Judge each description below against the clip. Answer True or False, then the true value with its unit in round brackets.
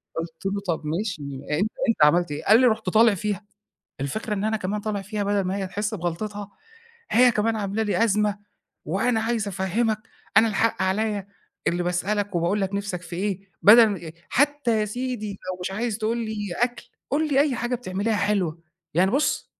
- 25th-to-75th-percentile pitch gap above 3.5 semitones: False (2.9 semitones)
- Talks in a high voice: True (205 Hz)